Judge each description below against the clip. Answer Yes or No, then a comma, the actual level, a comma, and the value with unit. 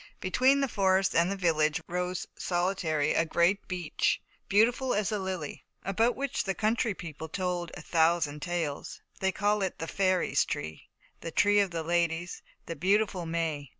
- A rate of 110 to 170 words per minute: Yes, average, 165 wpm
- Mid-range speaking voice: Yes, medium, 180 Hz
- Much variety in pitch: No, average, 3.2 semitones